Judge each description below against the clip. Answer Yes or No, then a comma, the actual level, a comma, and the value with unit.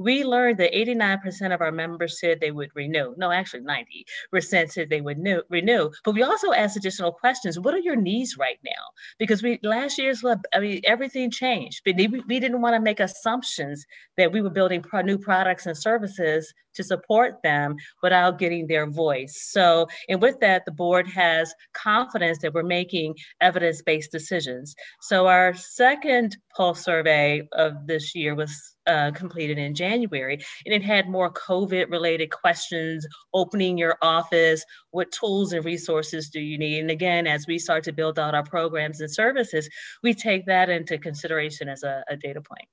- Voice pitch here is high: No, medium, 175 Hz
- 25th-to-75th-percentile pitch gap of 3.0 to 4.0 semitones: No, average, 4.7 semitones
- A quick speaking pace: No, average, 175 wpm